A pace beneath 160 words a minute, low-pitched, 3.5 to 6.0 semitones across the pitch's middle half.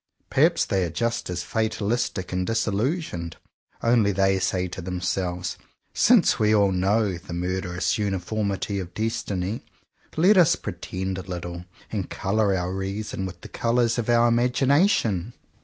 Yes: average, 140 wpm; low, 100 Hz; average, 3.8 semitones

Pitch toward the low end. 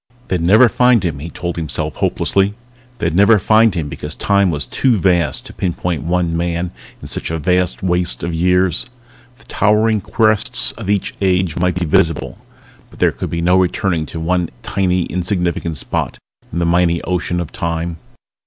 Yes: very low, 90 Hz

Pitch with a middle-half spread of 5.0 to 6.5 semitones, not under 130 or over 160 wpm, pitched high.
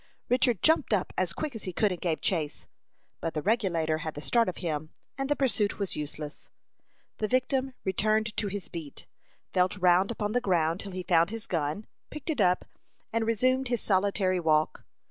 No: average, 5.3 semitones; average, 190 wpm; high, 195 Hz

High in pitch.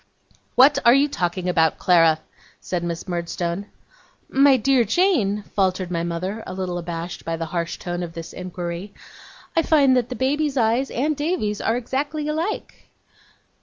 Yes: high, 200 Hz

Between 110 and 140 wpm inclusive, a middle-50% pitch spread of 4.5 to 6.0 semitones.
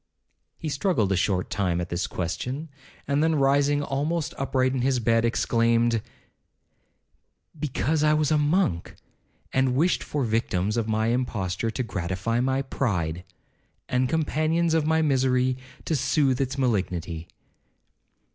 Yes: slow, 135 wpm; average, 5.3 semitones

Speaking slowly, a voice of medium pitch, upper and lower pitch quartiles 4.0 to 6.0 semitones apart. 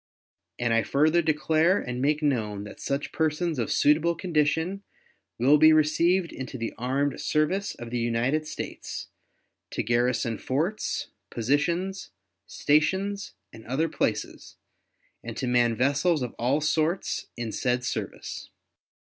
Yes: slow, 130 wpm; medium, 145 Hz; average, 4.9 semitones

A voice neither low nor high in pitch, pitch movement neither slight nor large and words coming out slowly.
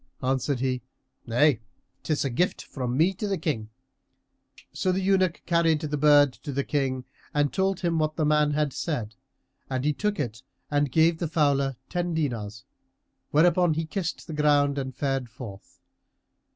No: medium, 145 Hz; average, 3.8 semitones; average, 165 wpm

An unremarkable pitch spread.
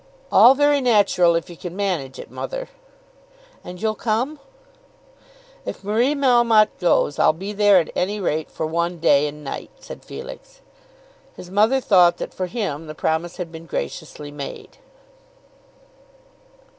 No: wide, 5.7 semitones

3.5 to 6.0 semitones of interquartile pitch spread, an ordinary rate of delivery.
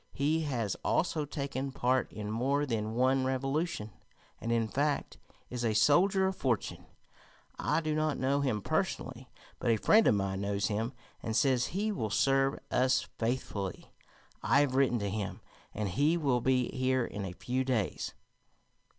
Yes: average, 4.3 semitones; average, 165 wpm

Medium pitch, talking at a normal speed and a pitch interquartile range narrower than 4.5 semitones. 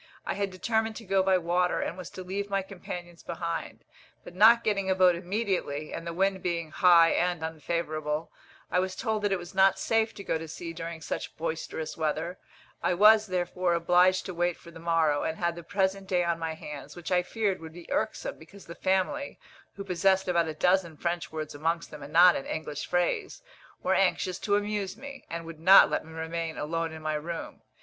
No: medium, 175 Hz; fast, 210 wpm; average, 2.8 semitones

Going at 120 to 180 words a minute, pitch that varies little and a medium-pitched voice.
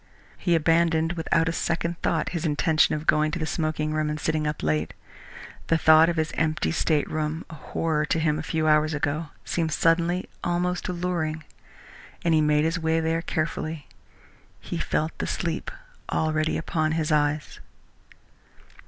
Yes: average, 160 wpm; narrow, 1.3 semitones; medium, 160 Hz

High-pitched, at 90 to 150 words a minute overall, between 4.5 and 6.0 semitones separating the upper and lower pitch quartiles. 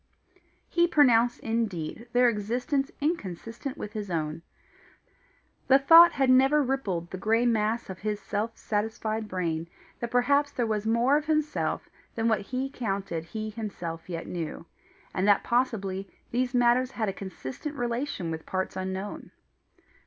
Yes: high, 225 Hz; average, 145 wpm; average, 4.9 semitones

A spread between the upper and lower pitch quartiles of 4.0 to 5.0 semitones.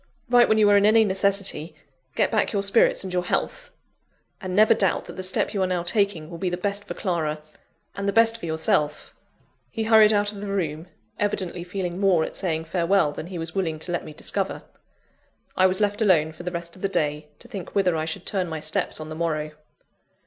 No: average, 3.6 semitones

